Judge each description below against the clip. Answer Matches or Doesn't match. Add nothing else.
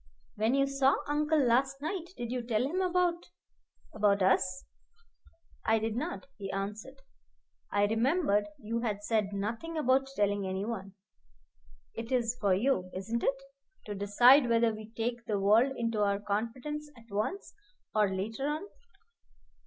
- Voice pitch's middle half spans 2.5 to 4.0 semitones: Doesn't match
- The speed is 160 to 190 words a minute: Doesn't match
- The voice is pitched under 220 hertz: Doesn't match